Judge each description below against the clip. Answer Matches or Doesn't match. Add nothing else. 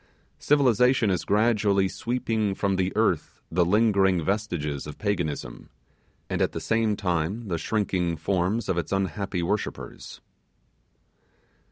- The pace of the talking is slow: Matches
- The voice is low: Matches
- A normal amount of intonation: Matches